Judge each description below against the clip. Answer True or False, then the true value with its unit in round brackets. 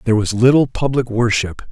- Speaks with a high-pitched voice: False (120 Hz)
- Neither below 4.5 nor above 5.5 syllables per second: False (5.8 syllables/s)